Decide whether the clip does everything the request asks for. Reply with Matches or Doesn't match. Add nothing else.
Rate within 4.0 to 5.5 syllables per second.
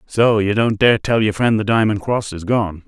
Matches